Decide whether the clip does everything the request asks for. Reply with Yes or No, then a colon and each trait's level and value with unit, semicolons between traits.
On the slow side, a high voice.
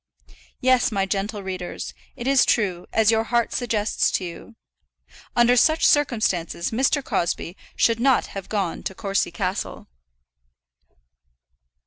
Yes: slow, 125 wpm; high, 215 Hz